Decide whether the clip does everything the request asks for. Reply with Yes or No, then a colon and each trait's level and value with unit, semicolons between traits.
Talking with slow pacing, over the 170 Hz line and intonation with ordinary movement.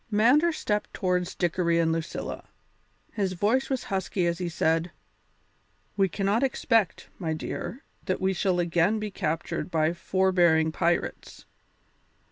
Yes: slow, 130 wpm; medium, 185 Hz; average, 3.5 semitones